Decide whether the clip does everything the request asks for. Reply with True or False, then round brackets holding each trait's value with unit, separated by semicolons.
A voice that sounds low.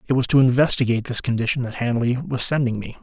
True (125 Hz)